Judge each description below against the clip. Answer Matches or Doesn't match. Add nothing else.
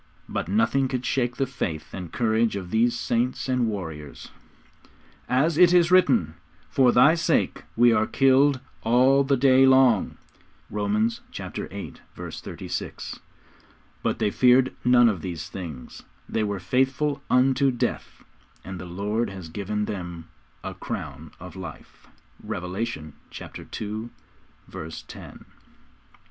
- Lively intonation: Matches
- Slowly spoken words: Matches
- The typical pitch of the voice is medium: Doesn't match